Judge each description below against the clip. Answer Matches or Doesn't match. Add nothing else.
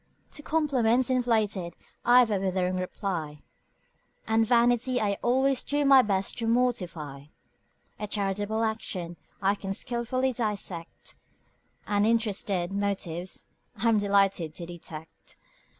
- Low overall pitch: Doesn't match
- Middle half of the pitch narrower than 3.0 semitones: Doesn't match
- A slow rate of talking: Matches